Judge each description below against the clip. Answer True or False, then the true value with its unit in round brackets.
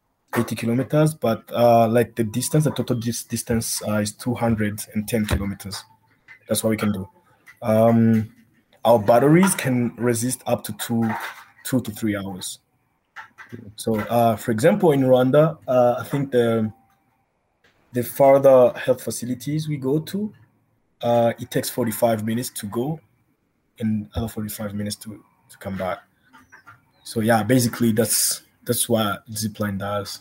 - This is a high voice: False (115 Hz)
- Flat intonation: True (2.2 semitones)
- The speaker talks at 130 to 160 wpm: True (140 wpm)